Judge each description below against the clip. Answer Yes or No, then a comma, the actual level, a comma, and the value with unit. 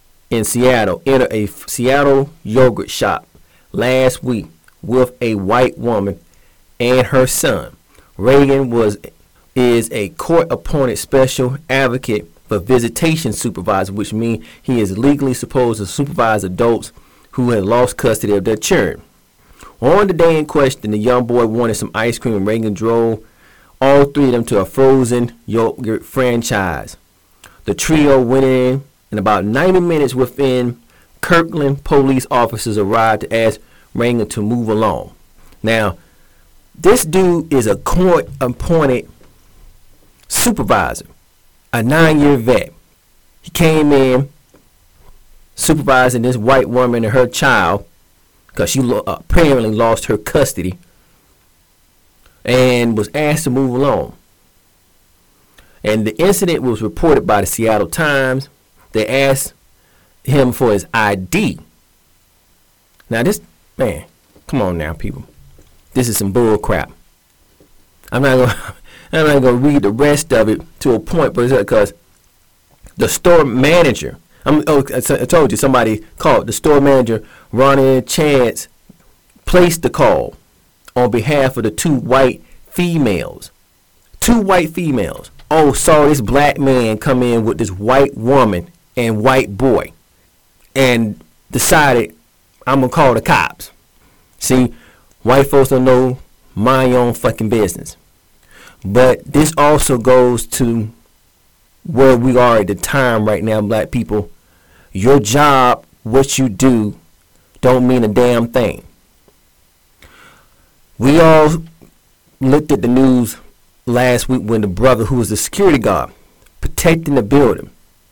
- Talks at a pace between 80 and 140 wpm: Yes, slow, 135 wpm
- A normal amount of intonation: Yes, average, 4.7 semitones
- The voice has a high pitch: No, low, 120 Hz